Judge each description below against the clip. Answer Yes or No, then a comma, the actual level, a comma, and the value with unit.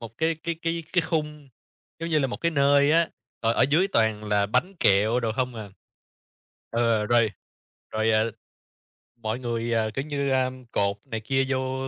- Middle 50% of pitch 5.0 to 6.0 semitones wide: Yes, average, 5.3 semitones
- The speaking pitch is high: No, low, 125 Hz